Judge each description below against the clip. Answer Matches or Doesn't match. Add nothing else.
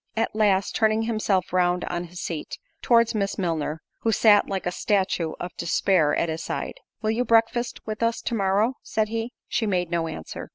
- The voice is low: Doesn't match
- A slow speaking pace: Doesn't match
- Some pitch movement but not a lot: Matches